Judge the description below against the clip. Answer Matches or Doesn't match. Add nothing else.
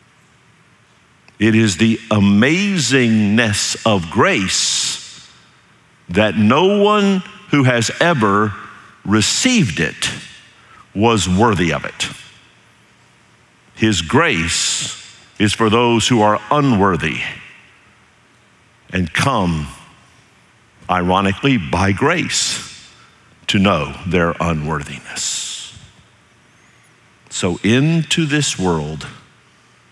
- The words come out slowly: Matches